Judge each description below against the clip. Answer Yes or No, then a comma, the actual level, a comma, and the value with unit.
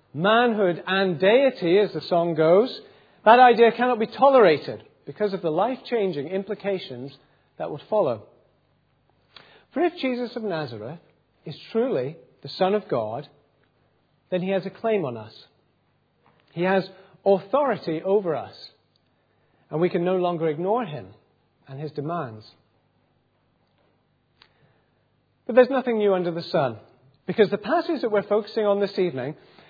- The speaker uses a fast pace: No, average, 140 wpm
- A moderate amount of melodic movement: No, wide, 5.9 semitones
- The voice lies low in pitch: No, high, 190 Hz